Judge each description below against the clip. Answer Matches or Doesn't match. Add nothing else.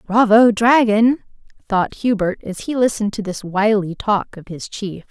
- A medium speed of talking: Matches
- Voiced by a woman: Matches